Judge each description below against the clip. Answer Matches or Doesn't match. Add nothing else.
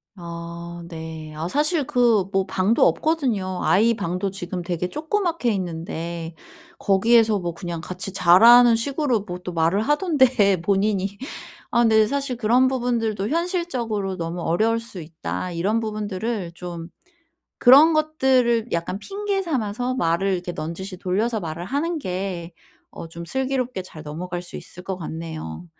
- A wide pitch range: Matches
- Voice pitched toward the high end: Matches